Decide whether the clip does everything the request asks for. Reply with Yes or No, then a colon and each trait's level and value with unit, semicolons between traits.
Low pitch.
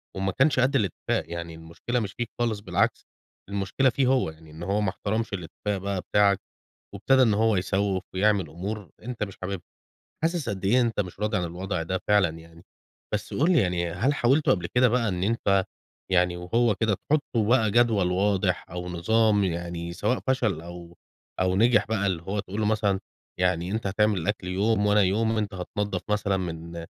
Yes: low, 100 Hz